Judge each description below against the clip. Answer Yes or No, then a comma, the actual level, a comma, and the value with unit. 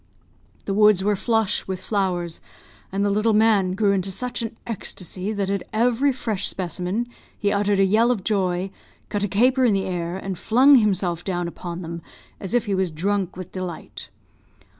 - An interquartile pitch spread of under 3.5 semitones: Yes, average, 2.9 semitones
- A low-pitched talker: No, high, 200 Hz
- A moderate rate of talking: Yes, average, 180 wpm